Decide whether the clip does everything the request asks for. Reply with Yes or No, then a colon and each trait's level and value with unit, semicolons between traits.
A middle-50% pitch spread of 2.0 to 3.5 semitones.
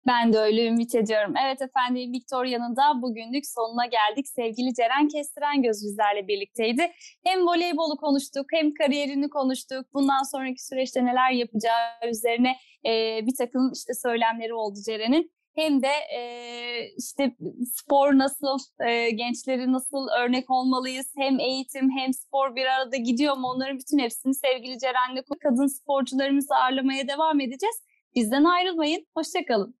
Yes: average, 2.7 semitones